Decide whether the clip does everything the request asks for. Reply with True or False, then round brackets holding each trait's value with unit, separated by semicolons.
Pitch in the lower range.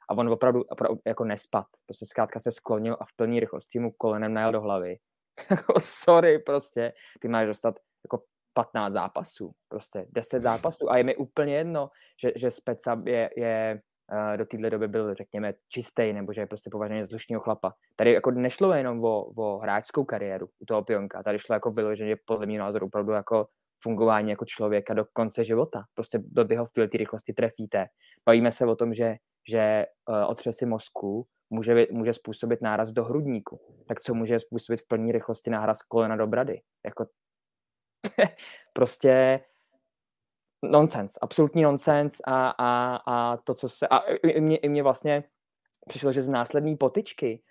True (115 Hz)